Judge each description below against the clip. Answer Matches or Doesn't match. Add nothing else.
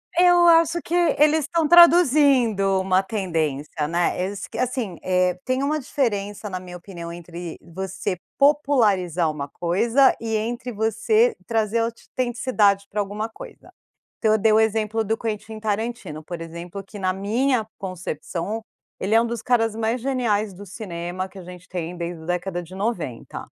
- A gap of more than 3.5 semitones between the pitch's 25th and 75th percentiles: Matches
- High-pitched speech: Matches